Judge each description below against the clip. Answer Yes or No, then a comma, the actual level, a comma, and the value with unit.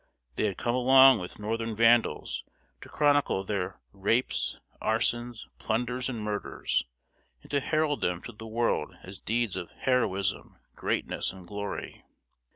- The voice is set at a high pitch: No, low, 115 Hz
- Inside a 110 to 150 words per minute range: Yes, average, 140 wpm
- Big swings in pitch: No, average, 3.4 semitones